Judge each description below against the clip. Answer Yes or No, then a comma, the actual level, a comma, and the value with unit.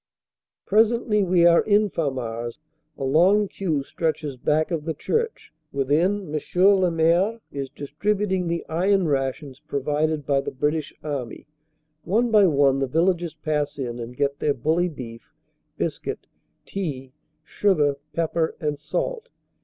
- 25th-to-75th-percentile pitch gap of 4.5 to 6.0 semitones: Yes, average, 5.2 semitones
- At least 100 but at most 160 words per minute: Yes, average, 145 wpm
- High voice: No, medium, 155 Hz